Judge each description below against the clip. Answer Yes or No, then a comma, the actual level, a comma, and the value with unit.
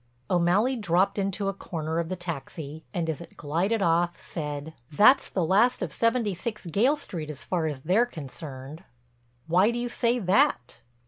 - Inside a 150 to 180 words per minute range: Yes, average, 170 wpm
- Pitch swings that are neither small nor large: Yes, average, 4.6 semitones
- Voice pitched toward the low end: No, medium, 175 Hz